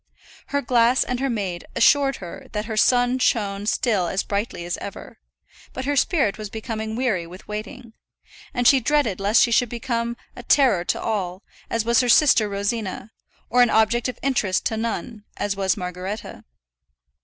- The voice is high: Yes, high, 225 Hz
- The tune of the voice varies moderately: Yes, average, 3.5 semitones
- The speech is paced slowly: No, average, 175 wpm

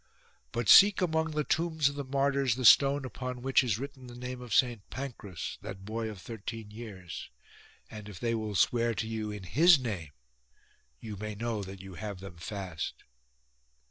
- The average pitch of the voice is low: Yes, low, 115 Hz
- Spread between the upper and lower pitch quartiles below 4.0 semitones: No, average, 4.7 semitones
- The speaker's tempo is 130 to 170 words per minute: No, average, 180 wpm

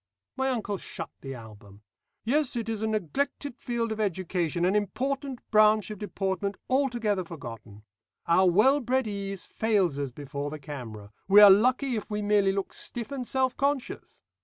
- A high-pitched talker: Yes, high, 205 Hz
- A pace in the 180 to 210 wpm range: No, average, 165 wpm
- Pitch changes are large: Yes, wide, 6.1 semitones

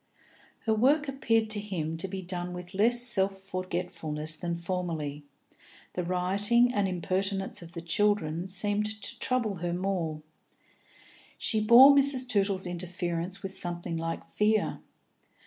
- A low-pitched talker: No, high, 190 Hz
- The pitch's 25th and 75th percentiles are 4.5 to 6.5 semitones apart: No, average, 3.5 semitones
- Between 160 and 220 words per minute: No, slow, 135 wpm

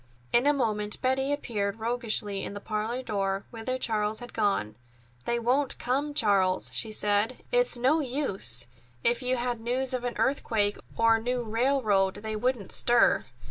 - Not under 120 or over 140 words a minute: No, average, 165 wpm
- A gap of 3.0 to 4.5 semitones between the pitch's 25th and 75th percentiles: Yes, average, 3.5 semitones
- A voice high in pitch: Yes, high, 230 Hz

